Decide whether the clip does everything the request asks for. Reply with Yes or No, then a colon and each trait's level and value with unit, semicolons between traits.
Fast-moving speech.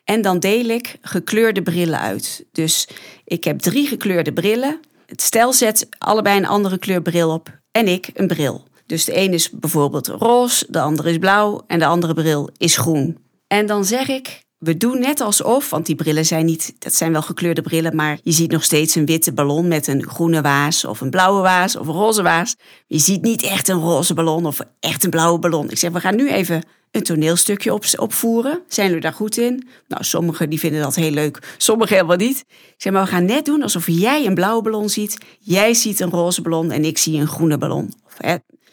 Yes: fast, 220 wpm